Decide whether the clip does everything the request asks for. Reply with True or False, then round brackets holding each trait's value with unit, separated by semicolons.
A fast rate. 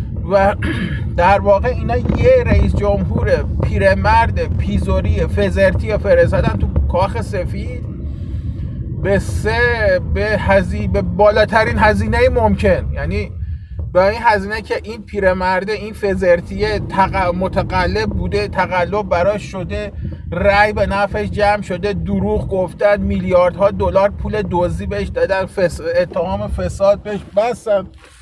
False (110 wpm)